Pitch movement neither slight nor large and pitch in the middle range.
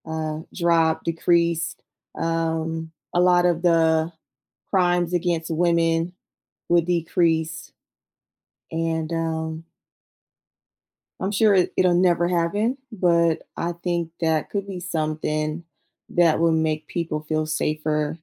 No: narrow, 1.5 semitones; medium, 165 Hz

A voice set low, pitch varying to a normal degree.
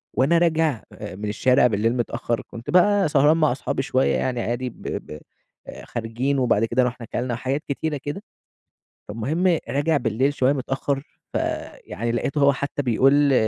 Yes: low, 130 Hz; average, 3.6 semitones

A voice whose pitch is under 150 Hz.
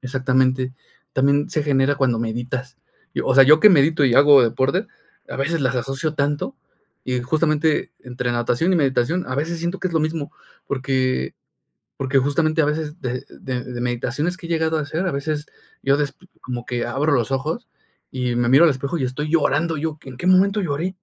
Yes: medium, 140 Hz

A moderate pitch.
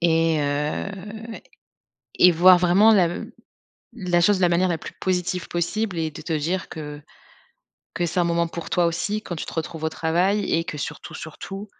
Yes: medium, 175 Hz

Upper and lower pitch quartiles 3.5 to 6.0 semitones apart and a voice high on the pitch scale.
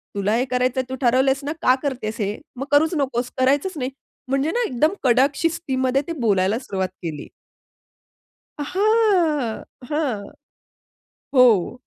Yes: average, 3.8 semitones; very high, 260 Hz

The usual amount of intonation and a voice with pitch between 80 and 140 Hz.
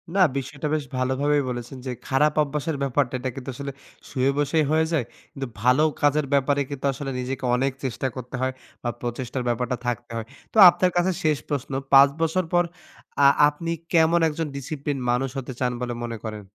Yes: average, 3.0 semitones; low, 135 Hz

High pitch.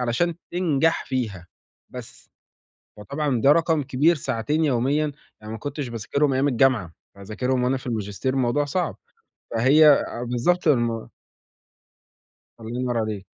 No: low, 130 Hz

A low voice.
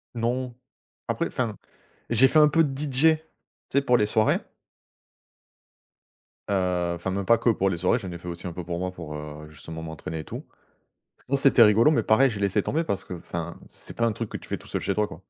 Yes: low, 105 Hz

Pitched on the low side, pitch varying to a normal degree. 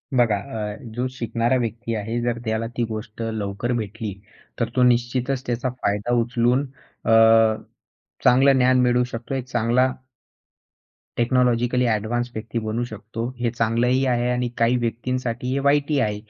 No: low, 120 Hz; narrow, 1.9 semitones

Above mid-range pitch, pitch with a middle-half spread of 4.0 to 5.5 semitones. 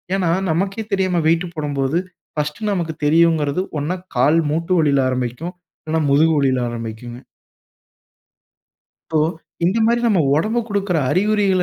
No: medium, 160 Hz; average, 4.7 semitones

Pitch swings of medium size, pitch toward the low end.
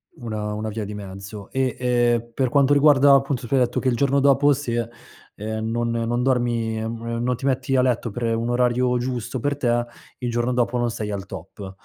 No: narrow, 2.3 semitones; low, 120 Hz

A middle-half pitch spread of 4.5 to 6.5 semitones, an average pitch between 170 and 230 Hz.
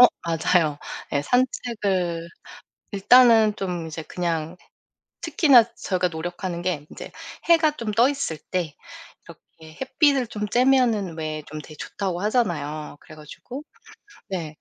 No: wide, 6.9 semitones; medium, 185 Hz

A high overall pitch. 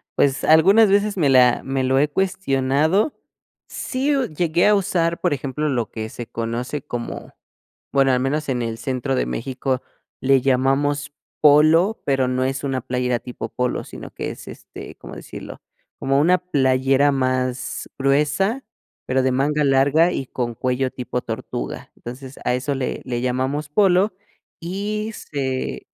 No: low, 135 Hz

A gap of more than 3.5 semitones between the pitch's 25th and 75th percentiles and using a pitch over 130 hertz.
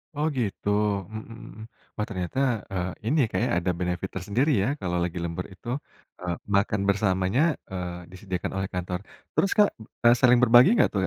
No: average, 4.1 semitones; very low, 95 Hz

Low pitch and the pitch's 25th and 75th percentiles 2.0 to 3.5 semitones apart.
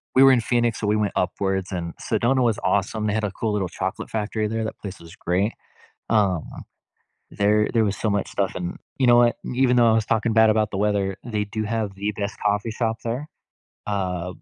Yes: low, 105 Hz; narrow, 2.4 semitones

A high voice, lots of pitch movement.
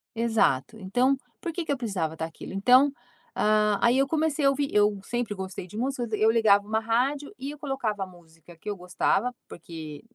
Yes: high, 220 Hz; wide, 6.1 semitones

